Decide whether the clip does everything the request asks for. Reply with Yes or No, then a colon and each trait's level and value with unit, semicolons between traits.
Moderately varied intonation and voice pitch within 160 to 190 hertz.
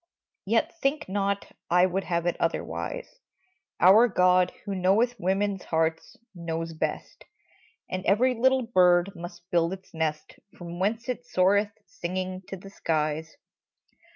Yes: average, 3.0 semitones; medium, 185 Hz